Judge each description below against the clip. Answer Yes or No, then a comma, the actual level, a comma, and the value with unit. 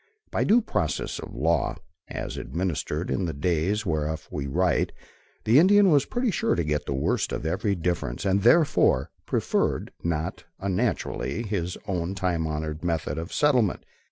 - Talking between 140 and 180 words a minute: Yes, average, 155 wpm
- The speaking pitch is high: No, very low, 85 Hz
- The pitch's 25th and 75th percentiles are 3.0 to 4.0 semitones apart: No, average, 5.0 semitones